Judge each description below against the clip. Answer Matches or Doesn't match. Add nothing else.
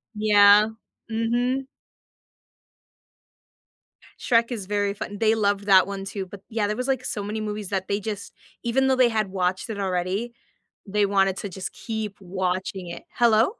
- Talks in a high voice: Matches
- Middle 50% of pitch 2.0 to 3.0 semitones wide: Matches